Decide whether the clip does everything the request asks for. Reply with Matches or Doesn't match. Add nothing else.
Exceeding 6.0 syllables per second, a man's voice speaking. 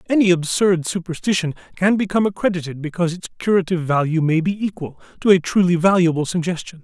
Matches